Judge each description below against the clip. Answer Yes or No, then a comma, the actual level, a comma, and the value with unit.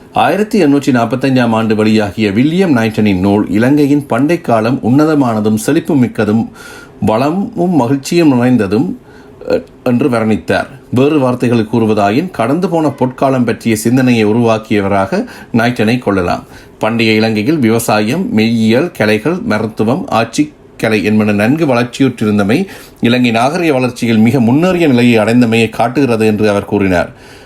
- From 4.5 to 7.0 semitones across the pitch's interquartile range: No, average, 3.7 semitones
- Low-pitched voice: Yes, low, 115 Hz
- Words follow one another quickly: No, average, 110 wpm